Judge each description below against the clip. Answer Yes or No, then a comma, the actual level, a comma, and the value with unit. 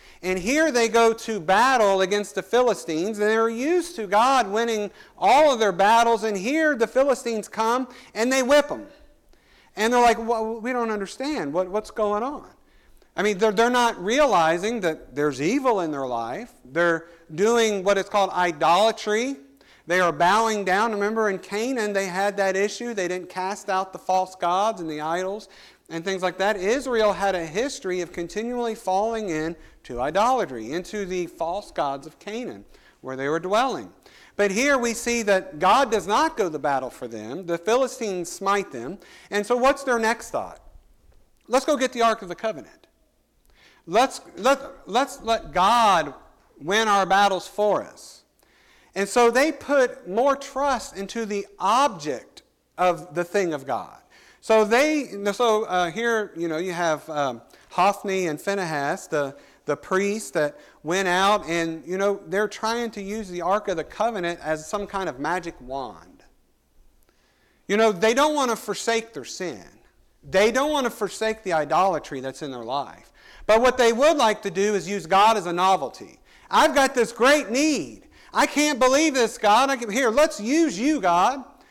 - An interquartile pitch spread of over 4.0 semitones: Yes, average, 4.6 semitones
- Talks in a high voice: Yes, high, 210 Hz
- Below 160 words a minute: No, average, 180 wpm